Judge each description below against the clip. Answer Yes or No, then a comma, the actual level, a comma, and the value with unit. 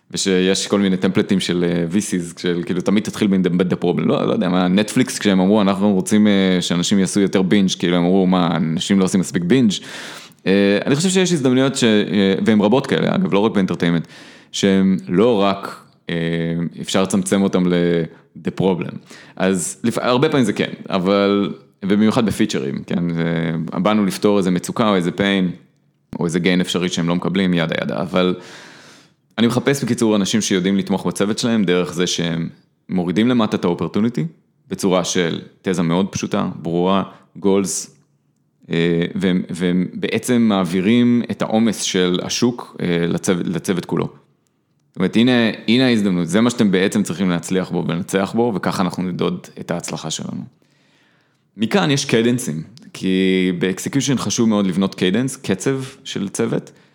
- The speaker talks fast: Yes, fast, 160 wpm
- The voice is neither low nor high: No, very low, 95 Hz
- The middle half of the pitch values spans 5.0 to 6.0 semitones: No, average, 3.3 semitones